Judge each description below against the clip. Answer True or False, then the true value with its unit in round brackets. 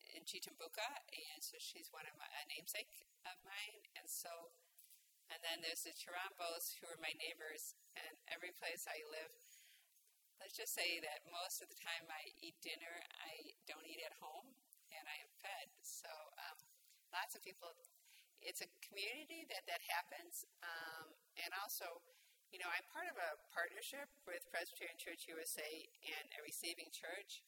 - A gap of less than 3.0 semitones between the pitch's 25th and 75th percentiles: False (4.4 semitones)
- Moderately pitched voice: True (170 Hz)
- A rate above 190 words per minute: False (170 wpm)